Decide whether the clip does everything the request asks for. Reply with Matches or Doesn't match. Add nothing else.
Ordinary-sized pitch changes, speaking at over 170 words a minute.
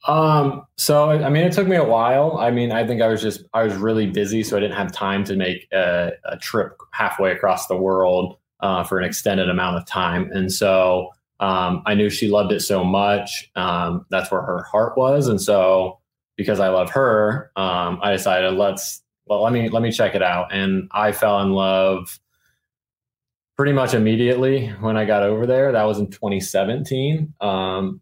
Matches